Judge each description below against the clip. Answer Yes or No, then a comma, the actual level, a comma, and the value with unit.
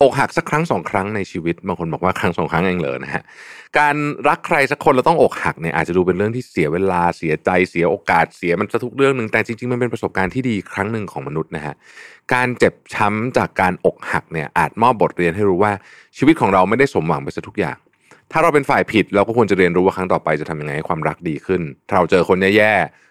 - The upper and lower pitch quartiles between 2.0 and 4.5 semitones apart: No, average, 5.3 semitones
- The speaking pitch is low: Yes, low, 105 Hz